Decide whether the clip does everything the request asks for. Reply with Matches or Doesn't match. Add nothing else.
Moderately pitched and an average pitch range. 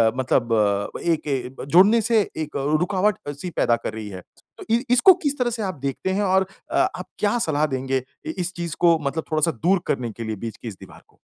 Doesn't match